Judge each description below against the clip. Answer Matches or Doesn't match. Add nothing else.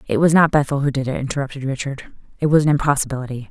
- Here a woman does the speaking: Matches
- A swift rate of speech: Matches